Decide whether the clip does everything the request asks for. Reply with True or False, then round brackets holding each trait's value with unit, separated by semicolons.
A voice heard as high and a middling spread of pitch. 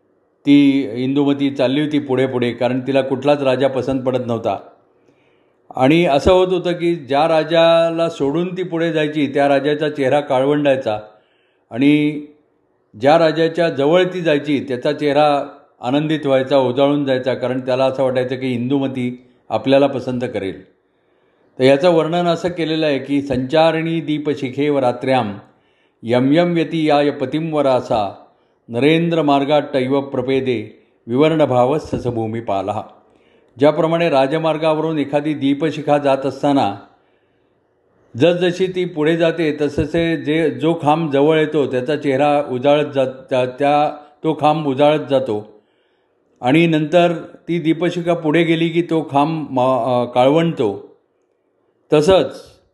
False (145 Hz; 3.5 semitones)